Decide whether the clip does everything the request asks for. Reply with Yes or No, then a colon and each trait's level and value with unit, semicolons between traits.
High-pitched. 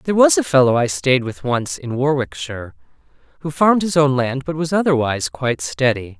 No: low, 135 Hz